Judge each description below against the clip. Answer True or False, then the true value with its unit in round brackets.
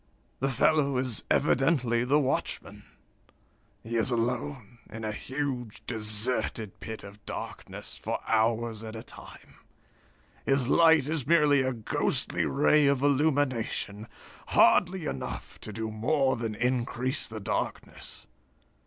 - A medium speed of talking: False (125 wpm)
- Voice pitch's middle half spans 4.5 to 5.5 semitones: False (3.9 semitones)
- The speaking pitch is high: False (125 Hz)